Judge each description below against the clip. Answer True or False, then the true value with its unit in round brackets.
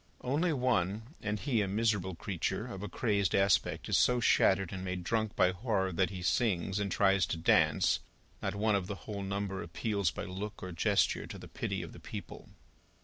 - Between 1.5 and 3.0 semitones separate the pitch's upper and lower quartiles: True (2.7 semitones)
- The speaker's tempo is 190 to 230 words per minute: True (200 wpm)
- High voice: False (100 Hz)